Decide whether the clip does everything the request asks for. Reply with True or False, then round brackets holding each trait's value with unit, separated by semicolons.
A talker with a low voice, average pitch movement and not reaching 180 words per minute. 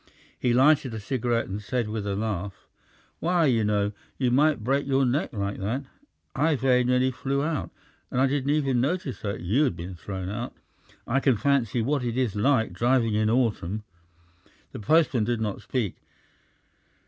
True (125 Hz; 4.3 semitones; 170 wpm)